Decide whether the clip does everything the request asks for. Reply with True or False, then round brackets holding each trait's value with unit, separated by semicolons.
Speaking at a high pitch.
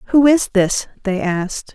True (215 Hz)